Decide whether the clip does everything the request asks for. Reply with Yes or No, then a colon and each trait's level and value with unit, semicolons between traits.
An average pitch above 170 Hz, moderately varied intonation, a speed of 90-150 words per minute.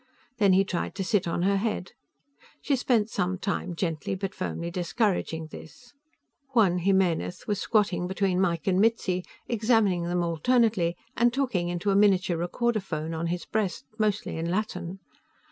No: high, 190 Hz; average, 3.4 semitones; average, 160 wpm